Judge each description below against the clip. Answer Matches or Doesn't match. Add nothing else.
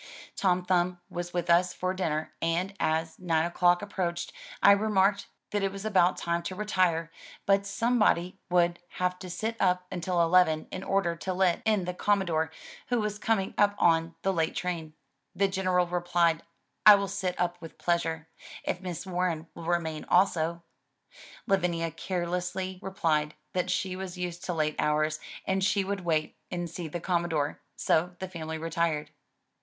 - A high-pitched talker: Doesn't match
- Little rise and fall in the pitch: Matches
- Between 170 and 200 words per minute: Matches